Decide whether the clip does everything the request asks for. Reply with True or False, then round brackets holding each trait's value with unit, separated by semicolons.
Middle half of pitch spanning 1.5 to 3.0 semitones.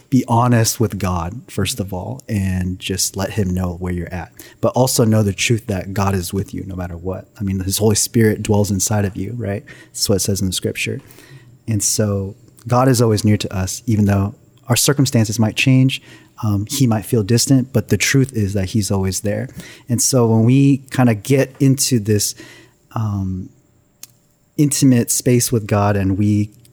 False (3.9 semitones)